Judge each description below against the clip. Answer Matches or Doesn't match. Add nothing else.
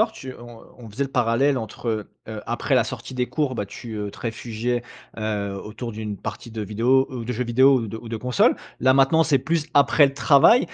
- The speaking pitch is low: Matches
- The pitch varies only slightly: Doesn't match